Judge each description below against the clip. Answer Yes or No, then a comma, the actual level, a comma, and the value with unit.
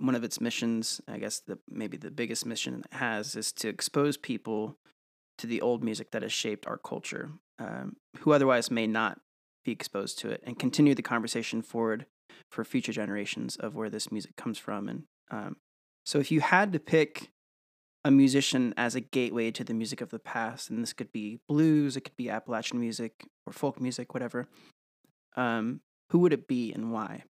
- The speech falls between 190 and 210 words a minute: Yes, average, 195 wpm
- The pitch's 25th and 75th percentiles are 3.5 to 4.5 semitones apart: Yes, average, 3.9 semitones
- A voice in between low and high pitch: No, low, 120 Hz